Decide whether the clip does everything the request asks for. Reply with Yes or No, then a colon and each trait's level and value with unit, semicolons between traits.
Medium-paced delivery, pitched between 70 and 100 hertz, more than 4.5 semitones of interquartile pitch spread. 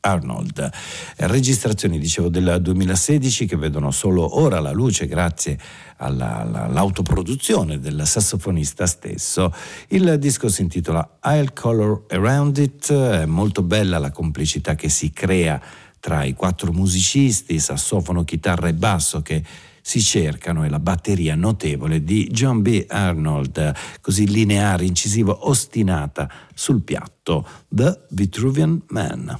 Yes: average, 125 wpm; very low, 95 Hz; wide, 5.6 semitones